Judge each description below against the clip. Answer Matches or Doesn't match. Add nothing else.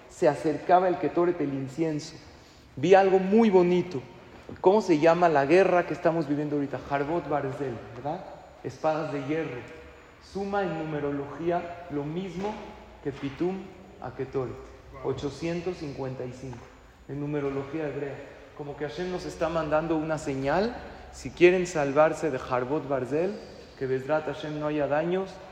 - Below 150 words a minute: Matches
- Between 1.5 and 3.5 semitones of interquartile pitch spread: Doesn't match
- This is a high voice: Doesn't match